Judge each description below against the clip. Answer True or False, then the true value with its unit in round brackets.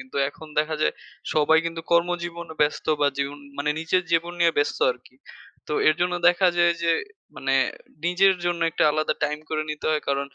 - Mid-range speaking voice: True (160 Hz)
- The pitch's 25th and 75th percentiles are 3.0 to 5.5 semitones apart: False (2.6 semitones)